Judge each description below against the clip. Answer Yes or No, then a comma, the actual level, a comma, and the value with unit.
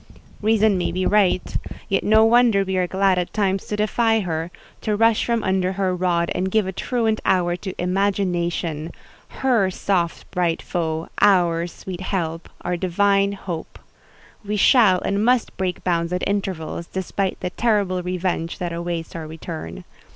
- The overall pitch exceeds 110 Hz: Yes, medium, 185 Hz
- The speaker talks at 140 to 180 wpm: Yes, average, 160 wpm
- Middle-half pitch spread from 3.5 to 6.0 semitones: No, average, 2.7 semitones